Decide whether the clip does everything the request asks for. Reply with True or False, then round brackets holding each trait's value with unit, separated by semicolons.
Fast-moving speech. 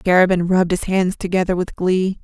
False (190 wpm)